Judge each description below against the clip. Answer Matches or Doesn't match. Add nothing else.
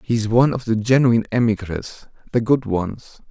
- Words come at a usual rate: Matches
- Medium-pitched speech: Doesn't match